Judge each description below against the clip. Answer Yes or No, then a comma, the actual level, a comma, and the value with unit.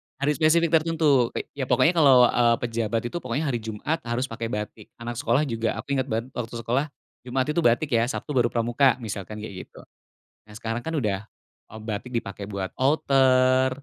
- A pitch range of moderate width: Yes, average, 3.7 semitones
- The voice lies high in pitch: No, low, 120 Hz